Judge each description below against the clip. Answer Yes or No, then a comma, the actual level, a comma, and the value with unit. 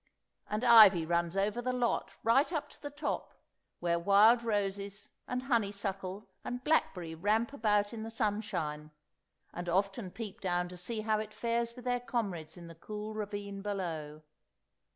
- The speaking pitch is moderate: No, high, 205 Hz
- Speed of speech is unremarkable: Yes, average, 160 wpm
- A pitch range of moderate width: Yes, average, 4.2 semitones